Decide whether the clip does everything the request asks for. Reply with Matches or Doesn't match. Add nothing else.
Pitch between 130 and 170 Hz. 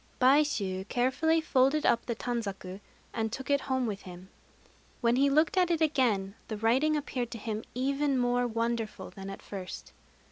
Doesn't match